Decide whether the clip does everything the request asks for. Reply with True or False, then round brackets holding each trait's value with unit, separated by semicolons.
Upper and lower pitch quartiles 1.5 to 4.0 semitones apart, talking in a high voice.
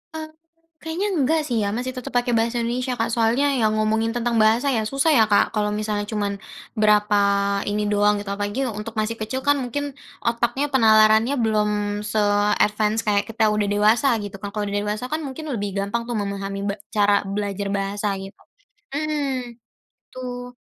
True (3.1 semitones; 220 Hz)